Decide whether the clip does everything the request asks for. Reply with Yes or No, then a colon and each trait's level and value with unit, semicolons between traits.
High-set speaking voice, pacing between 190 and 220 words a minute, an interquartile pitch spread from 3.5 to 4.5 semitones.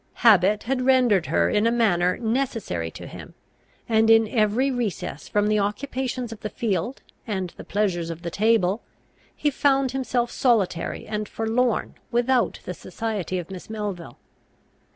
No: high, 220 Hz; average, 150 wpm; average, 4.2 semitones